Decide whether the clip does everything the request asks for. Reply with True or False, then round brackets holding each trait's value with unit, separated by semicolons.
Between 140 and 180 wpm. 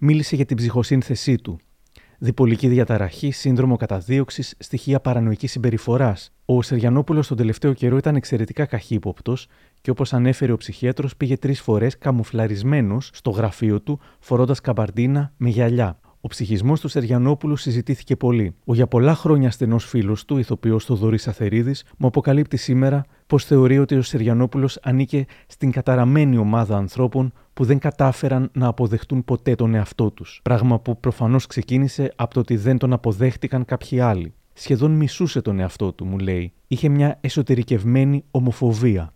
True (150 wpm)